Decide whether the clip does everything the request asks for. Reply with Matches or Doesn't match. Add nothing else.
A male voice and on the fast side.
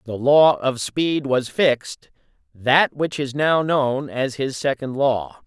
Doesn't match